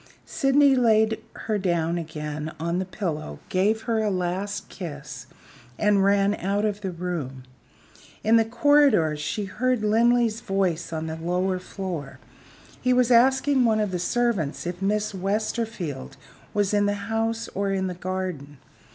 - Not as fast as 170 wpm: Yes, average, 150 wpm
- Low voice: No, high, 195 Hz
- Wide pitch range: No, average, 4.4 semitones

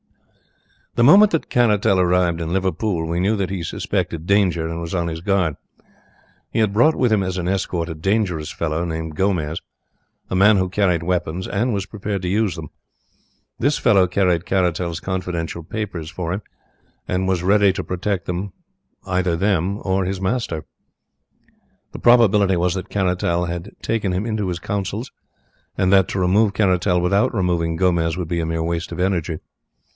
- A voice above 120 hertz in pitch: No, very low, 90 Hz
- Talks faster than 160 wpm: Yes, average, 170 wpm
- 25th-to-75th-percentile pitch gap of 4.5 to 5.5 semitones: No, average, 2.7 semitones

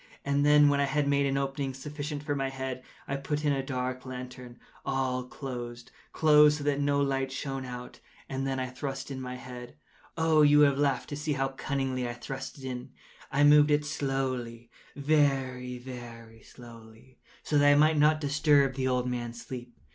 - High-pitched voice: No, low, 135 Hz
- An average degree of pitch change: No, narrow, 2.3 semitones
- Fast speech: No, average, 185 wpm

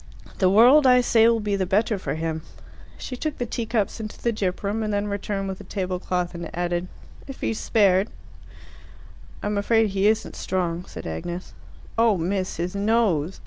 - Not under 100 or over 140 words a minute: No, average, 180 wpm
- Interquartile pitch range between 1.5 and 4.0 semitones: Yes, average, 3.5 semitones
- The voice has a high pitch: Yes, high, 200 Hz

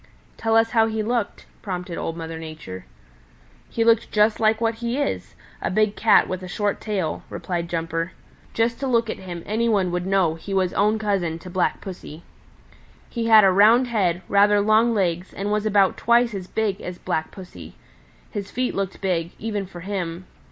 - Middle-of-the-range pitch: No, high, 200 Hz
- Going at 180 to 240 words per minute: Yes, average, 190 wpm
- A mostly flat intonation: No, average, 3.9 semitones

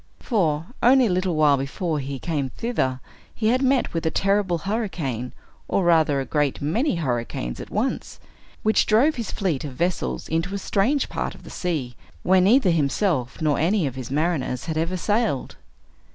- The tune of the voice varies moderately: No, wide, 6.2 semitones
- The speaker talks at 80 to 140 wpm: No, average, 180 wpm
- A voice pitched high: No, medium, 170 Hz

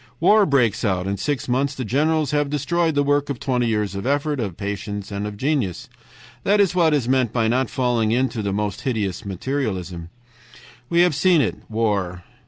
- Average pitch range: No, wide, 5.9 semitones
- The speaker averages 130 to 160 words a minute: No, average, 190 wpm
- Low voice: Yes, low, 125 Hz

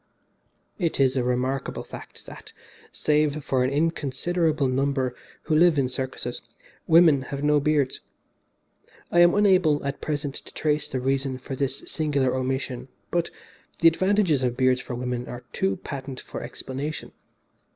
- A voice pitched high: No, medium, 140 Hz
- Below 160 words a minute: Yes, average, 150 wpm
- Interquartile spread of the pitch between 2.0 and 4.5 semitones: Yes, average, 3.0 semitones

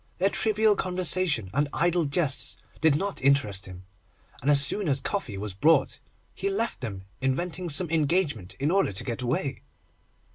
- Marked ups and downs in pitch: Yes, wide, 6.1 semitones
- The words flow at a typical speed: Yes, average, 160 wpm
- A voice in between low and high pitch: Yes, medium, 145 Hz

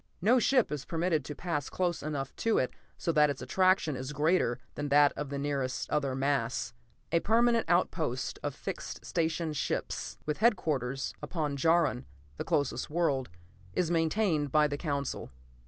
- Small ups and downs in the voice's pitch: No, average, 3.6 semitones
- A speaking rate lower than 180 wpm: Yes, average, 160 wpm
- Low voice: No, medium, 150 Hz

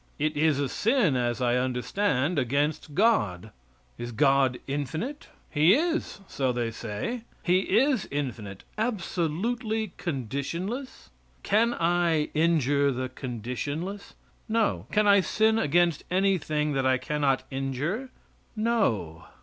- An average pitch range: No, wide, 7.7 semitones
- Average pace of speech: No, slow, 115 wpm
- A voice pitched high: No, medium, 150 Hz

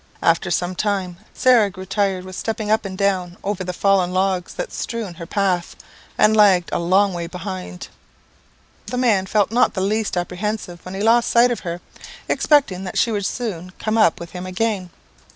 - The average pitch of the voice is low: No, high, 190 Hz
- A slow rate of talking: No, average, 190 wpm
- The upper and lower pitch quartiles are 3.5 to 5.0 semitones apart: No, average, 3.0 semitones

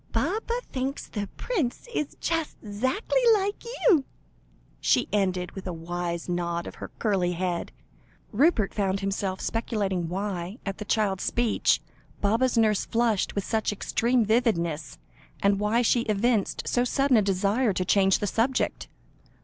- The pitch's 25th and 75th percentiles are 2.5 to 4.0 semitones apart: No, average, 4.5 semitones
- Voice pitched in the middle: No, high, 210 Hz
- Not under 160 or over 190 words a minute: No, average, 145 wpm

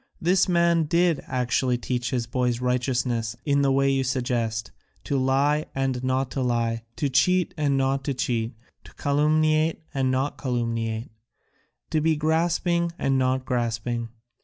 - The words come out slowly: No, average, 155 wpm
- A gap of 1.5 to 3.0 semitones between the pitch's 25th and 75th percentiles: No, average, 3.6 semitones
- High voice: No, low, 130 Hz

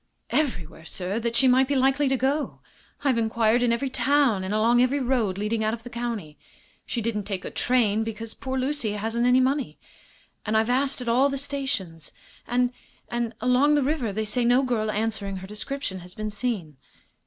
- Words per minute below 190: No, average, 195 wpm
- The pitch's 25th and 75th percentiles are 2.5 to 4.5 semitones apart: Yes, average, 3.6 semitones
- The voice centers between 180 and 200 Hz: No, high, 235 Hz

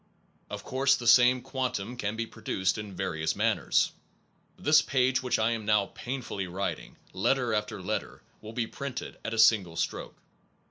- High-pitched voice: No, low, 115 Hz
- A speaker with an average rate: Yes, average, 160 wpm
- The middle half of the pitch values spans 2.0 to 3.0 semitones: No, average, 4.2 semitones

